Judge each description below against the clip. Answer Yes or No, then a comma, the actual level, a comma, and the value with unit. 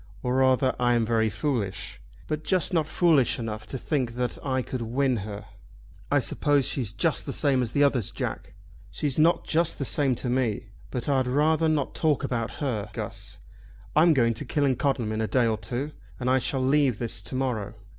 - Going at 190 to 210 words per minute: Yes, average, 195 wpm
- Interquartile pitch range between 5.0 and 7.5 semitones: No, average, 3.7 semitones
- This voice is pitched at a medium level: No, low, 130 Hz